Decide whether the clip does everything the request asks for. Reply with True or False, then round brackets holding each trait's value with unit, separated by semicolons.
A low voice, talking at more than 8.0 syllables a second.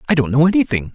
False (150 Hz; 8.2 syllables/s)